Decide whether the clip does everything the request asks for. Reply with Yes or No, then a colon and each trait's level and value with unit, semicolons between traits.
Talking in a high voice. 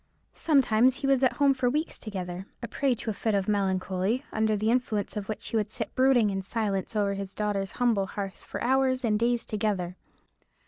Yes: high, 215 Hz